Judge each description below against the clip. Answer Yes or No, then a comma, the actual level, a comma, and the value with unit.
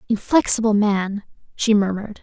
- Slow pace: Yes, slow, 110 wpm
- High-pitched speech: Yes, high, 210 Hz